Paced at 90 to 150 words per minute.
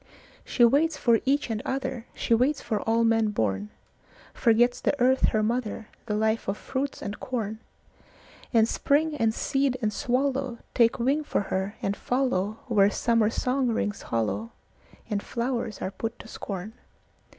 Yes: slow, 135 wpm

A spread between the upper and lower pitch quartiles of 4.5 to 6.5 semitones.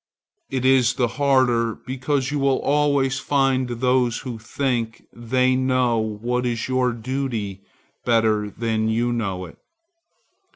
No: narrow, 2.5 semitones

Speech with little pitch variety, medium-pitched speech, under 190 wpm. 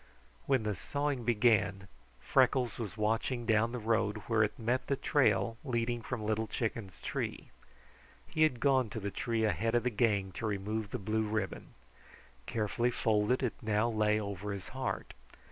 No: narrow, 2.3 semitones; low, 110 Hz; average, 165 wpm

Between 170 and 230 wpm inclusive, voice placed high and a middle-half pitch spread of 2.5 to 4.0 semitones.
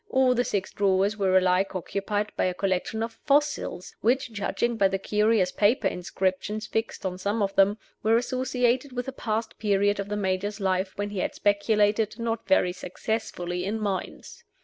Yes: average, 175 wpm; high, 205 Hz; average, 2.9 semitones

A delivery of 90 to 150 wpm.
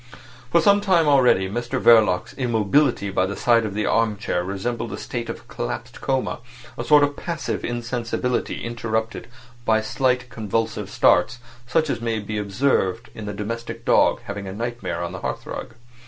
No: average, 160 wpm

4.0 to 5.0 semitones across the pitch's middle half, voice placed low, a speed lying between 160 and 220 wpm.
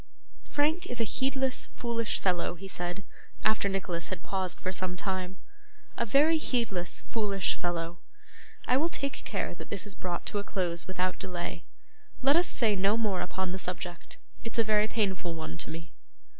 No: average, 4.4 semitones; high, 195 Hz; average, 175 wpm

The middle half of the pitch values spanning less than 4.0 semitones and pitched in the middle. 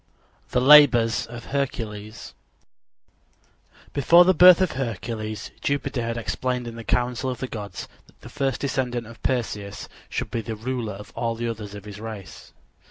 No: average, 3.1 semitones; low, 120 Hz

